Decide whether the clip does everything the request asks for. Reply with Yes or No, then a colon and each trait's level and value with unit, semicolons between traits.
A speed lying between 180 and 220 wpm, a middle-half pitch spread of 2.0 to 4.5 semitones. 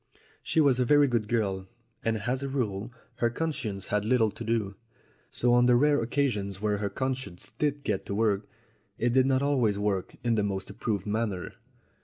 Yes: average, 190 wpm; average, 4.2 semitones